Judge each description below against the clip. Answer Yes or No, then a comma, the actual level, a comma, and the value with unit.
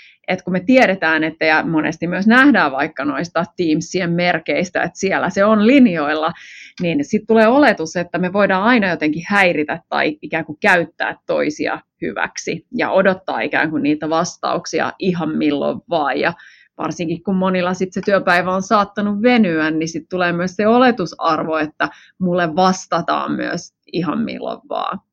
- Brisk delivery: Yes, fast, 160 wpm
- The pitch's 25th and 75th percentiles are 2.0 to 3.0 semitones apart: No, average, 3.7 semitones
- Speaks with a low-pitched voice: No, medium, 180 Hz